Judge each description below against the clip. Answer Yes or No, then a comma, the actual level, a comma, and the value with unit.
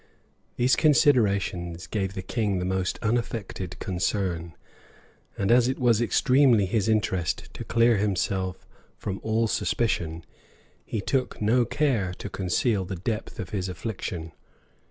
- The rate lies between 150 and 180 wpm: No, slow, 135 wpm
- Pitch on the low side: Yes, low, 100 Hz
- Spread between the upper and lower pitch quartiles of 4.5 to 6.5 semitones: No, average, 4.0 semitones